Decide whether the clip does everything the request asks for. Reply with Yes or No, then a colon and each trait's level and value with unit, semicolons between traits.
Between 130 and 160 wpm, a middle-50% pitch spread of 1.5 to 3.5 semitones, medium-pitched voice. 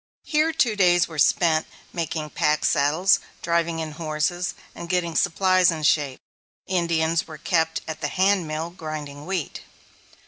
Yes: average, 140 wpm; average, 2.7 semitones; medium, 165 Hz